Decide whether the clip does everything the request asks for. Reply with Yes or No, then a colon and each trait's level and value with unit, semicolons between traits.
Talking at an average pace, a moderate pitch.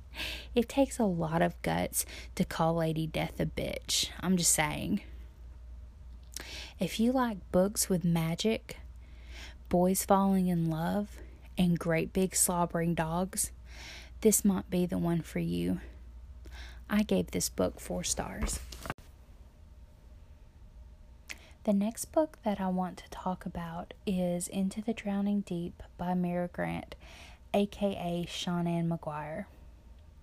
No: slow, 125 wpm; medium, 170 Hz